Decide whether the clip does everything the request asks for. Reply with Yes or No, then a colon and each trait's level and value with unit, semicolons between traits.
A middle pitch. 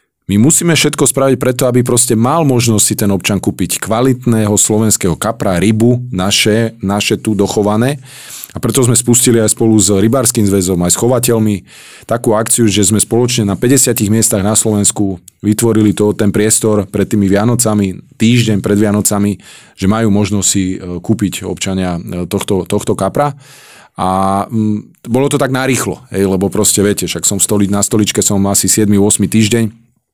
No: low, 105 Hz